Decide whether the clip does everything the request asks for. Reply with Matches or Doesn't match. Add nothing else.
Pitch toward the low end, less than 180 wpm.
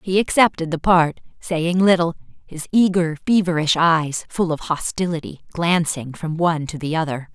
Doesn't match